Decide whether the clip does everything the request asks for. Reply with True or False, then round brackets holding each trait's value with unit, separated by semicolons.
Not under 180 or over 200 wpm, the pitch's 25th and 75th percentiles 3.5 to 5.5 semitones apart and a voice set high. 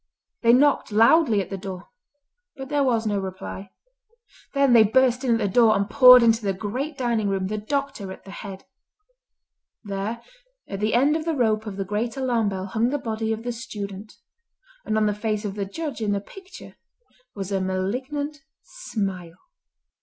True (185 wpm; 4.2 semitones; 220 Hz)